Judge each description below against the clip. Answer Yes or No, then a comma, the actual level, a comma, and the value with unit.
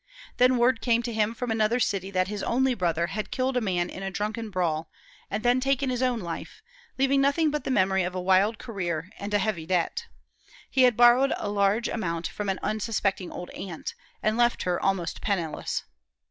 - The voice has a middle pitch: No, high, 210 Hz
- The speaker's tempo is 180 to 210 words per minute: Yes, average, 200 wpm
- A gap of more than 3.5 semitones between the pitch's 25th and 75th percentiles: Yes, average, 4.7 semitones